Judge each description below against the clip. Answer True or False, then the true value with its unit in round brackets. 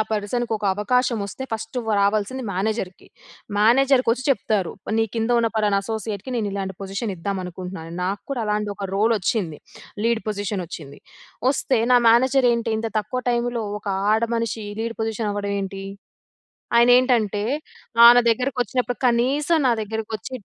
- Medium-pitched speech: False (220 Hz)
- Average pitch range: True (3.1 semitones)